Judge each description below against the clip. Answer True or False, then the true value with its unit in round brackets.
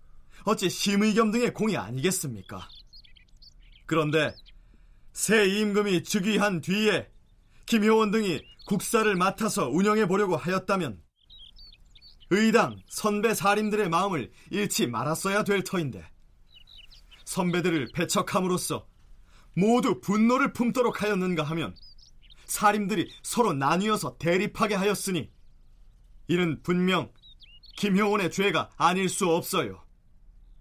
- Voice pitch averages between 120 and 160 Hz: False (180 Hz)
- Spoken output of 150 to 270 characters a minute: True (250 characters per minute)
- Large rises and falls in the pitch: True (8.2 semitones)